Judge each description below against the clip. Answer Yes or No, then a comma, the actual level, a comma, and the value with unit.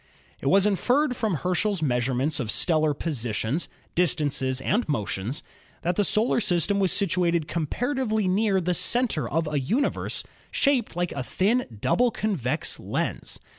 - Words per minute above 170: No, average, 140 wpm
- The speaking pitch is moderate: Yes, medium, 175 Hz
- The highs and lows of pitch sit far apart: Yes, wide, 6.6 semitones